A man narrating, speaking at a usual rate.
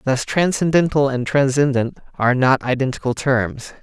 No: male; slow, 125 wpm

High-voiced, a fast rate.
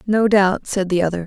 Yes: high, 195 Hz; fast, 240 wpm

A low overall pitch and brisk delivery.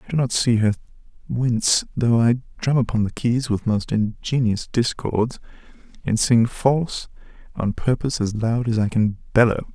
No: low, 115 Hz; average, 165 wpm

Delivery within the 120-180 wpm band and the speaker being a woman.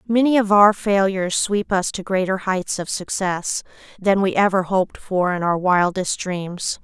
Yes: average, 175 wpm; female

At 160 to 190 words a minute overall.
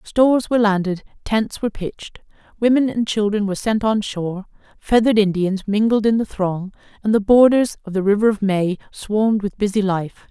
Yes: average, 180 wpm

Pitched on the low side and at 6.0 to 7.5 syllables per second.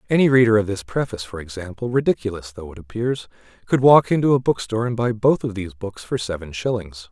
Yes: low, 110 Hz; 6.3 syllables/s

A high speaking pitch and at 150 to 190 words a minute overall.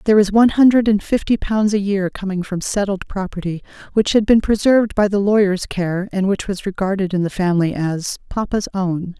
No: high, 195 Hz; average, 200 wpm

